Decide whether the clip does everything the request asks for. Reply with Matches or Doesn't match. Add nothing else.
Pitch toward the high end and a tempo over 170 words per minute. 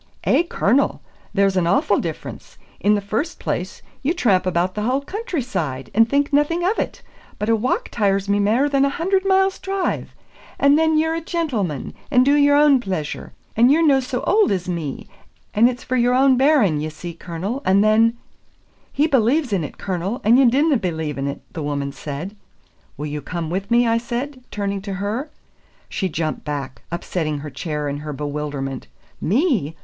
Matches